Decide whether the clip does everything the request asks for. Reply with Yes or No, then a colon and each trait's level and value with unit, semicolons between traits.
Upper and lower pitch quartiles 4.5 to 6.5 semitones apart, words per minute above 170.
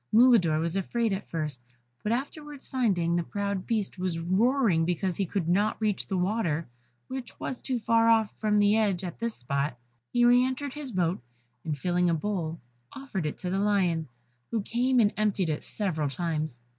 Yes: average, 5.3 semitones; average, 190 wpm